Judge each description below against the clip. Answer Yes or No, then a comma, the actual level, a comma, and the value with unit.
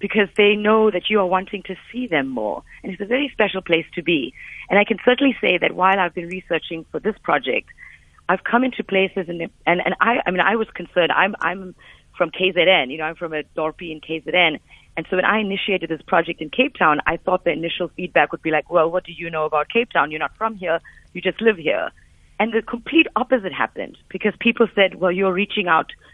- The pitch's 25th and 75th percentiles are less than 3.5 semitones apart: No, average, 4.3 semitones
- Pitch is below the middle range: No, medium, 185 Hz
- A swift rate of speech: Yes, fast, 235 wpm